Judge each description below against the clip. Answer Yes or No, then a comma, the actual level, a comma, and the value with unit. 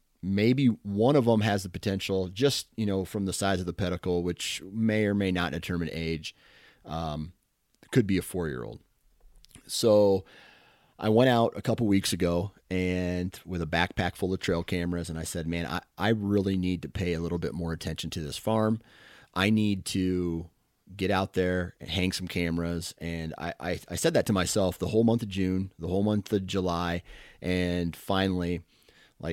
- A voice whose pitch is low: Yes, very low, 90 Hz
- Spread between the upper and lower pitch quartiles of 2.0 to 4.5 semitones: Yes, average, 2.8 semitones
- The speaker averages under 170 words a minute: No, average, 190 wpm